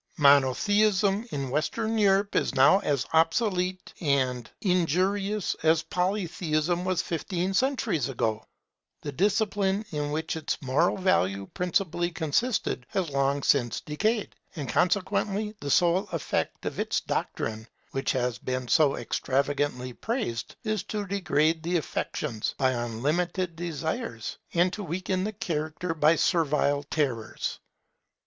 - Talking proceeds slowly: Yes, slow, 125 wpm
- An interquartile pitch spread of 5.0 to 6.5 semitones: Yes, wide, 5.5 semitones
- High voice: No, medium, 165 Hz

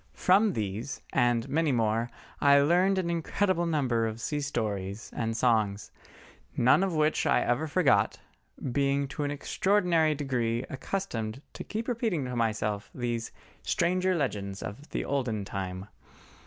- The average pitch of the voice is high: No, low, 135 Hz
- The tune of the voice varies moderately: No, wide, 6.6 semitones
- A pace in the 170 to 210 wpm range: No, average, 140 wpm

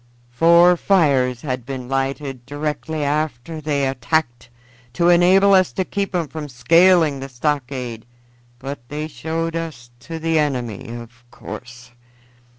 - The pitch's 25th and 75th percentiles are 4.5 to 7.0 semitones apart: Yes, average, 4.8 semitones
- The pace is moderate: No, slow, 130 wpm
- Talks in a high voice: No, medium, 145 Hz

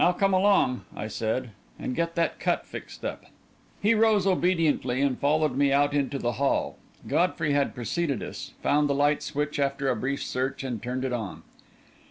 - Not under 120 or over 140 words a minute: No, average, 185 wpm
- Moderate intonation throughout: Yes, average, 4.5 semitones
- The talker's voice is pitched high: No, medium, 140 Hz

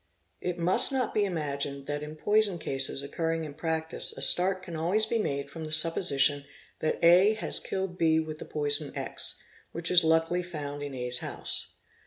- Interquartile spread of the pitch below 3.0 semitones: No, average, 3.6 semitones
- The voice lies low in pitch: No, medium, 160 Hz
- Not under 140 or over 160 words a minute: No, average, 185 wpm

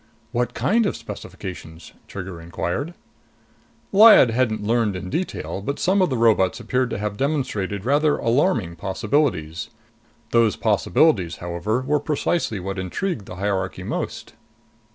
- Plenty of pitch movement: Yes, wide, 7.0 semitones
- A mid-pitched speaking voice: No, low, 110 Hz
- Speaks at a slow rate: Yes, slow, 130 wpm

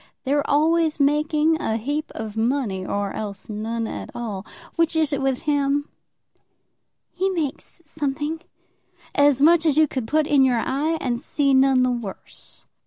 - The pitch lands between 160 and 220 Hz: No, very high, 280 Hz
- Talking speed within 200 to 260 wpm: No, average, 160 wpm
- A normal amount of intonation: Yes, average, 4.4 semitones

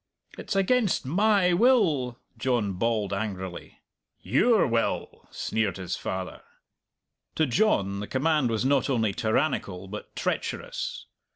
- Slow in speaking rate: Yes, slow, 115 wpm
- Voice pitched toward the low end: Yes, low, 120 Hz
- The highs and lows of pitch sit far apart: Yes, wide, 8.4 semitones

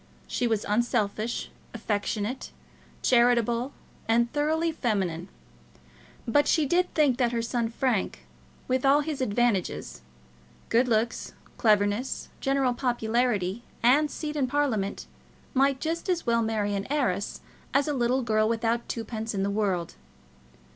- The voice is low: No, high, 235 Hz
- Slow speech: Yes, slow, 130 wpm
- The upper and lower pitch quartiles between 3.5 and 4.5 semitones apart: Yes, average, 3.8 semitones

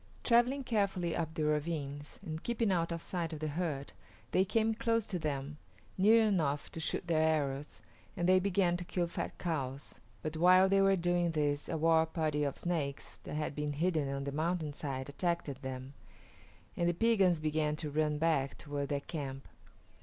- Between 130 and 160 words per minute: No, average, 185 wpm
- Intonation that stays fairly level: No, average, 3.6 semitones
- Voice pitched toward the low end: No, medium, 160 Hz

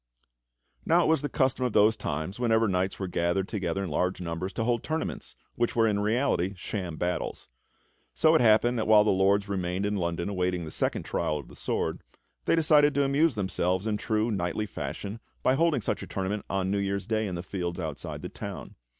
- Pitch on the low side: Yes, low, 100 Hz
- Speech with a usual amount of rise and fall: Yes, average, 4.2 semitones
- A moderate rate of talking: No, fast, 210 wpm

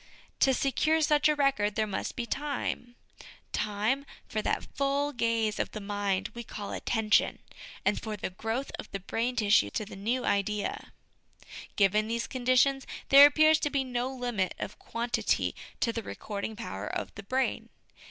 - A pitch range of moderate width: Yes, average, 4.3 semitones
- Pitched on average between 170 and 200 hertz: No, high, 230 Hz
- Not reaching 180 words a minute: Yes, average, 165 wpm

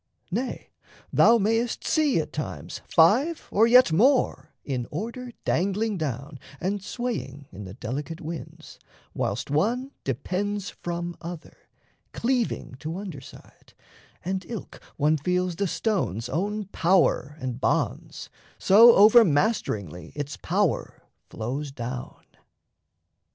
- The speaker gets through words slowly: Yes, slow, 120 wpm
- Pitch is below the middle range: No, medium, 175 Hz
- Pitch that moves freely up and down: Yes, wide, 7.3 semitones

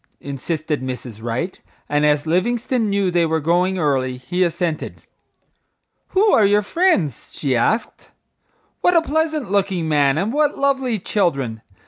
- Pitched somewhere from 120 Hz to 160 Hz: No, medium, 175 Hz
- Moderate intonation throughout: No, wide, 7.5 semitones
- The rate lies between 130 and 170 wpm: Yes, average, 140 wpm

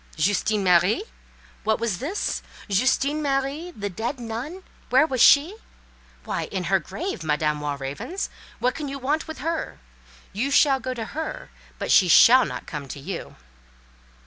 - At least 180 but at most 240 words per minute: No, average, 145 wpm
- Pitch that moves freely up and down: Yes, wide, 7.2 semitones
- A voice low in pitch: No, very high, 250 Hz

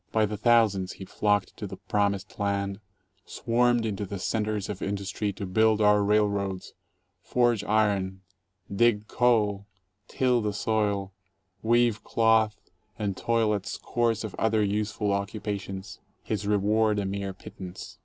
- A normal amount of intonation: No, narrow, 1.8 semitones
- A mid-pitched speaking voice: No, low, 105 Hz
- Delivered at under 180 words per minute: Yes, average, 140 wpm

